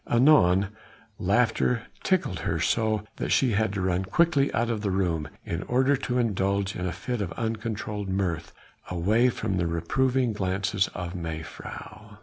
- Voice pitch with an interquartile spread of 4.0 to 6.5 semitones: Yes, average, 4.3 semitones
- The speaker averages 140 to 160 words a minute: Yes, average, 155 wpm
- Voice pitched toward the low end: Yes, low, 100 Hz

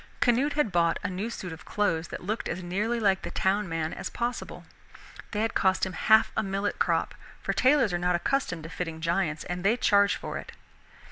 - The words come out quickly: Yes, fast, 210 wpm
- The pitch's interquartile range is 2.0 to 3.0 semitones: No, average, 4.1 semitones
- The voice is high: Yes, high, 195 Hz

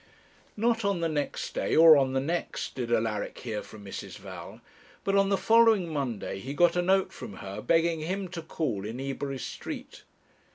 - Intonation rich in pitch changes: Yes, wide, 6.9 semitones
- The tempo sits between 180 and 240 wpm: Yes, average, 190 wpm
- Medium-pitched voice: Yes, medium, 155 Hz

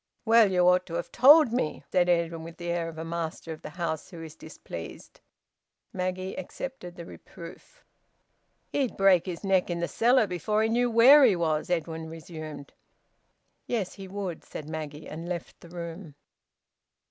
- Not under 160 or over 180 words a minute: Yes, average, 170 wpm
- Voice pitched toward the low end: No, medium, 175 Hz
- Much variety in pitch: No, average, 3.3 semitones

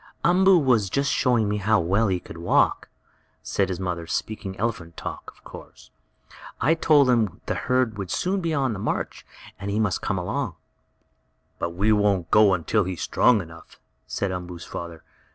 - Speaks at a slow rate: No, average, 185 wpm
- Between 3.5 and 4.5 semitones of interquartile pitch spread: No, wide, 5.5 semitones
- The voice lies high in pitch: No, low, 105 Hz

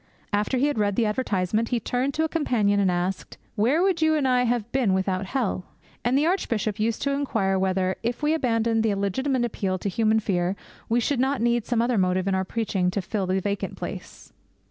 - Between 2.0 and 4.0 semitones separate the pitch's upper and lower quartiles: No, average, 4.7 semitones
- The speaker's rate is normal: No, fast, 215 wpm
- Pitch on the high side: Yes, high, 225 Hz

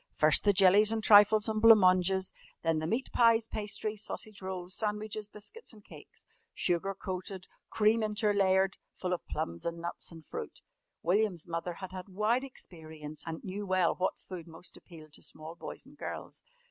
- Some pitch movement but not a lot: Yes, average, 3.7 semitones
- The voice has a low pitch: No, high, 190 Hz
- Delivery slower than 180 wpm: Yes, average, 170 wpm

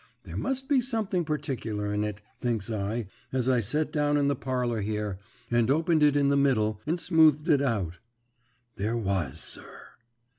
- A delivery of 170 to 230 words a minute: Yes, average, 175 wpm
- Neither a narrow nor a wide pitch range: No, wide, 6.1 semitones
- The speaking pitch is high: No, low, 130 Hz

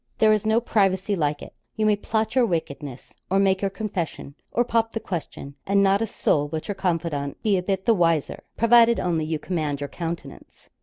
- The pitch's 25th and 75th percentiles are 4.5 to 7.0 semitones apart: Yes, average, 5.1 semitones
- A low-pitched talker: No, high, 190 Hz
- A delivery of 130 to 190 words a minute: No, fast, 205 wpm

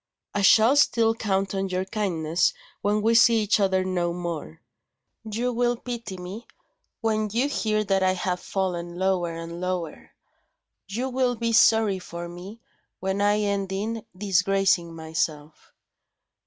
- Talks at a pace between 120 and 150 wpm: Yes, average, 145 wpm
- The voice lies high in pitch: Yes, high, 195 Hz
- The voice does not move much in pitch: No, average, 3.7 semitones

